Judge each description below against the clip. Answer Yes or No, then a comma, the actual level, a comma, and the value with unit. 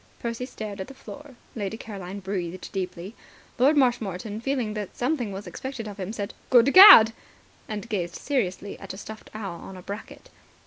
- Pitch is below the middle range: No, high, 215 Hz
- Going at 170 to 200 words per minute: Yes, average, 175 wpm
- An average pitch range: Yes, average, 4.1 semitones